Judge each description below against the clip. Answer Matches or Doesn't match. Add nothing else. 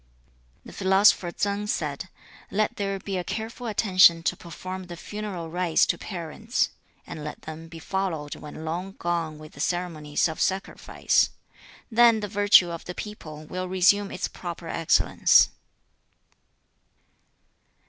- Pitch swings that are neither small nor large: Matches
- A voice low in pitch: Doesn't match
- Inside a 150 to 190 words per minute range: Doesn't match